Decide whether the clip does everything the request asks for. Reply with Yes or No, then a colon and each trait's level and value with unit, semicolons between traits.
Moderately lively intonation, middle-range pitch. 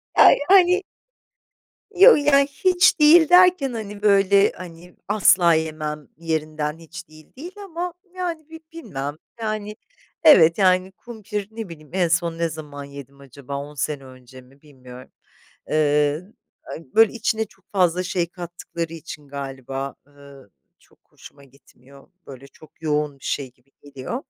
No: wide, 7.2 semitones; medium, 165 Hz